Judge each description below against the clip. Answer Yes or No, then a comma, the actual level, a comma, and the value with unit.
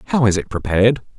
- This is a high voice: No, low, 110 Hz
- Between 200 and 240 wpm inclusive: Yes, fast, 205 wpm